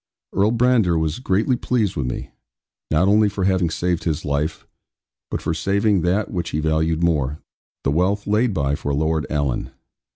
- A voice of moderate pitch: No, very low, 85 Hz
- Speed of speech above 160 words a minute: Yes, average, 170 wpm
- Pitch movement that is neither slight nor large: Yes, average, 4.7 semitones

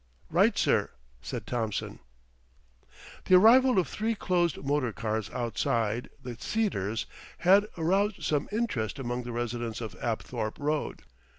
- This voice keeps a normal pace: No, slow, 125 wpm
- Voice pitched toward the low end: Yes, low, 125 Hz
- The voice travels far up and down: Yes, wide, 8.5 semitones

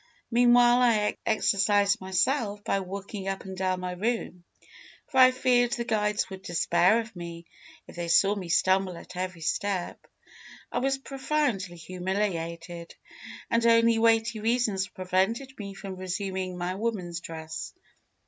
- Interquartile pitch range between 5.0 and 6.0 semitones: No, average, 4.0 semitones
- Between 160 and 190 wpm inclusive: No, average, 140 wpm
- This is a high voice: Yes, high, 195 Hz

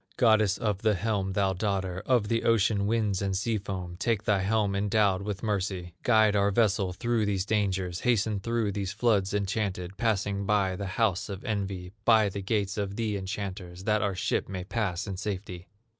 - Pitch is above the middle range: No, low, 100 Hz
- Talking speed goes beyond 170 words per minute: Yes, average, 185 wpm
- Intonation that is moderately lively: No, narrow, 2.2 semitones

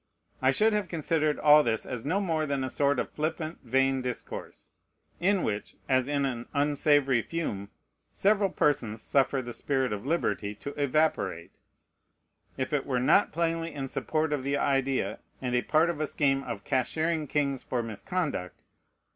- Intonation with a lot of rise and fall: No, average, 3.6 semitones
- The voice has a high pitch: No, medium, 140 Hz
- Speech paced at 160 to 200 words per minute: Yes, average, 165 wpm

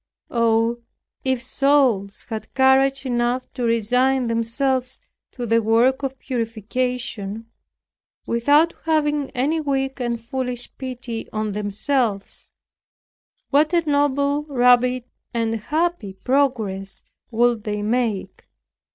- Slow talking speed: Yes, slow, 105 wpm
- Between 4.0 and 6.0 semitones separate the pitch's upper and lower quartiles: No, average, 3.0 semitones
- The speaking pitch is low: No, very high, 250 Hz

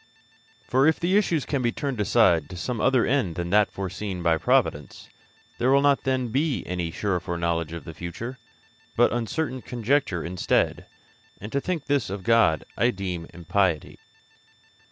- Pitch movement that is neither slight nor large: No, wide, 7.2 semitones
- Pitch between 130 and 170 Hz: No, low, 105 Hz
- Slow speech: No, average, 165 wpm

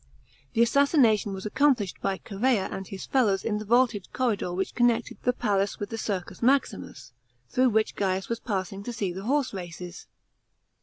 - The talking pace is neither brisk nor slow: Yes, average, 170 wpm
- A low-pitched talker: No, high, 210 Hz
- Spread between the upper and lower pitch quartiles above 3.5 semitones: Yes, average, 4.0 semitones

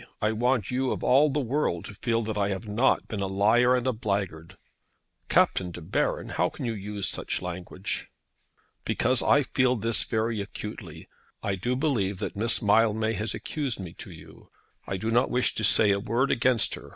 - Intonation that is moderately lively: Yes, average, 3.8 semitones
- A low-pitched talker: Yes, low, 110 Hz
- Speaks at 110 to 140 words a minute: No, average, 195 wpm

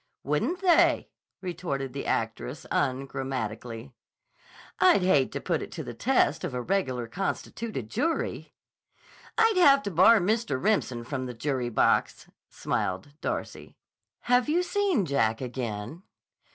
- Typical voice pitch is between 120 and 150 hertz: Yes, medium, 140 Hz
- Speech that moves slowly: Yes, slow, 130 wpm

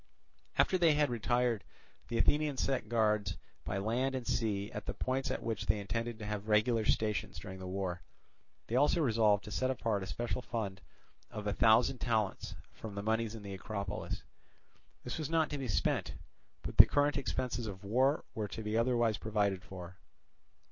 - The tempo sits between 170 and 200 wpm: Yes, average, 185 wpm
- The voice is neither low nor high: No, low, 110 Hz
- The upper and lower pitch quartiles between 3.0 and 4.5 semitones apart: Yes, average, 3.5 semitones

